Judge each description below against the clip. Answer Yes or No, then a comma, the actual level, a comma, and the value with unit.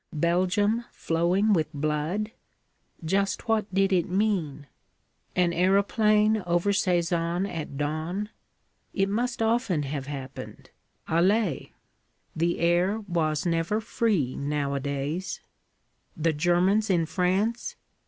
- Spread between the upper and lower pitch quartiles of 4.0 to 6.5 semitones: Yes, average, 4.5 semitones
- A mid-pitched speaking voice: Yes, medium, 180 Hz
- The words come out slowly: Yes, slow, 105 wpm